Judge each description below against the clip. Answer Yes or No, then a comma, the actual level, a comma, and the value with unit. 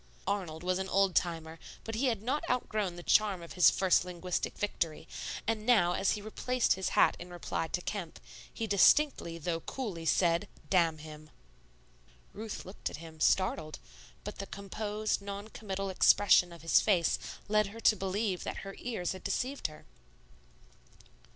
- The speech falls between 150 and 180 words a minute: Yes, average, 165 wpm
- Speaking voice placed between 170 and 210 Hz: Yes, high, 190 Hz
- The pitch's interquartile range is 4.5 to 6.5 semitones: No, average, 3.7 semitones